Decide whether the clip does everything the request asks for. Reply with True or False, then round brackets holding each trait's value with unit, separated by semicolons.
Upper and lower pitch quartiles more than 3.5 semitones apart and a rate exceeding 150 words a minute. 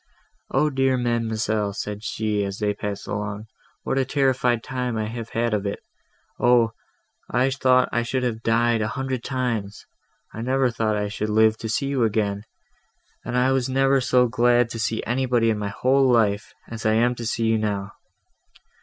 False (2.8 semitones; 185 wpm)